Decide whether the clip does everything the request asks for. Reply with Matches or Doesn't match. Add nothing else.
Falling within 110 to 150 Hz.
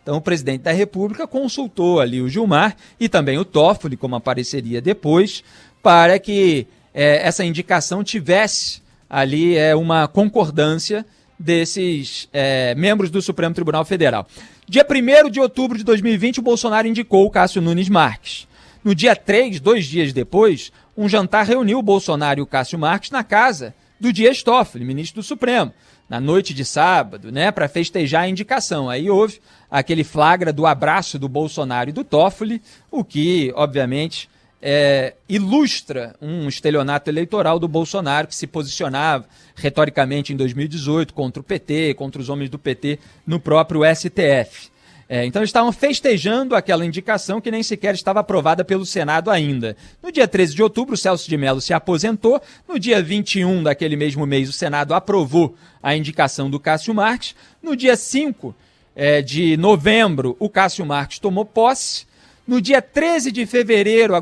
Doesn't match